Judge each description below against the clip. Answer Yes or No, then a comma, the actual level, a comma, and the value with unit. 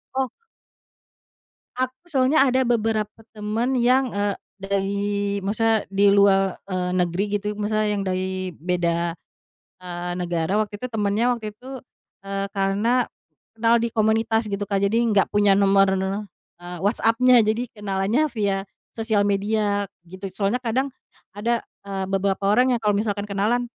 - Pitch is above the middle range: Yes, high, 205 Hz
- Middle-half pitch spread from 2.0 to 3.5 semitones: Yes, average, 2.7 semitones